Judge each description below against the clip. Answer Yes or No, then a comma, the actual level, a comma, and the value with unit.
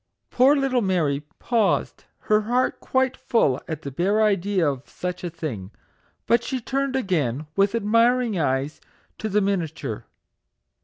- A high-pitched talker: Yes, high, 200 Hz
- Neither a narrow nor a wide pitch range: No, wide, 7.0 semitones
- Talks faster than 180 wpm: No, average, 145 wpm